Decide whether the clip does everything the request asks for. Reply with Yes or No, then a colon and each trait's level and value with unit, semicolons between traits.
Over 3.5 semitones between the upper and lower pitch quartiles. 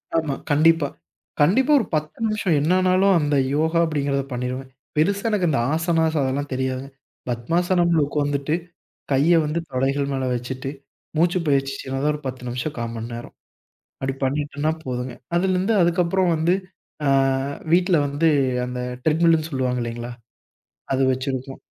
Yes: average, 4.4 semitones